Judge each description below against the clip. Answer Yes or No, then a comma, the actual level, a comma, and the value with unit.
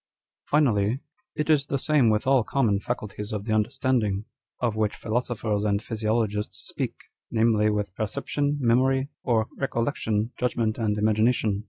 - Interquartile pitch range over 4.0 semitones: No, average, 3.3 semitones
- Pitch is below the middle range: Yes, low, 110 Hz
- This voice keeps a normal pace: Yes, average, 165 wpm